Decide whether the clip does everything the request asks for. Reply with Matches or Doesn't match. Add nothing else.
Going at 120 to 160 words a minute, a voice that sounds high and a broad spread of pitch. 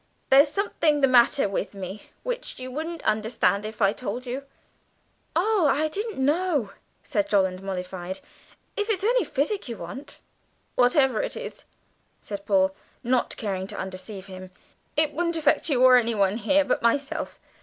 Matches